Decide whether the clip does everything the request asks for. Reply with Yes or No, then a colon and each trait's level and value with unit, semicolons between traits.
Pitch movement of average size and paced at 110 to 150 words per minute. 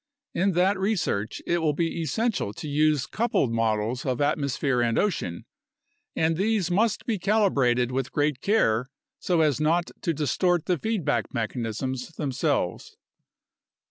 No: wide, 6.5 semitones; average, 140 wpm